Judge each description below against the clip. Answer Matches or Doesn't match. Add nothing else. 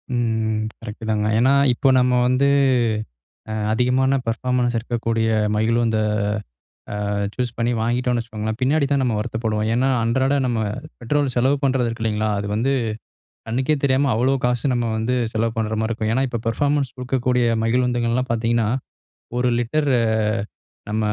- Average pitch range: Doesn't match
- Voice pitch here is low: Matches